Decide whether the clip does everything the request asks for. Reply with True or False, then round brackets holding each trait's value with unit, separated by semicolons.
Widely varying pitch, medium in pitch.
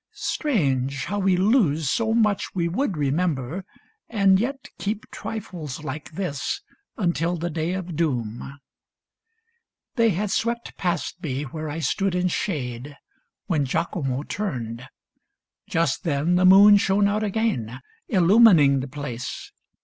True (6.0 semitones; 170 Hz)